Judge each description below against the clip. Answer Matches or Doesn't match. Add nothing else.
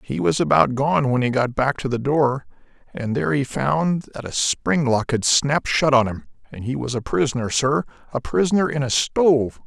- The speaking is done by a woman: Doesn't match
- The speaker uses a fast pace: Matches